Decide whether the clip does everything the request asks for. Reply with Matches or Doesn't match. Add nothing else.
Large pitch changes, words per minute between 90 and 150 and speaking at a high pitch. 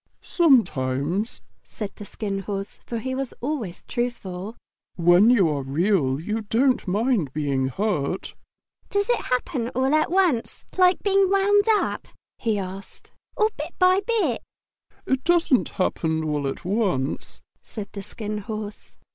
Matches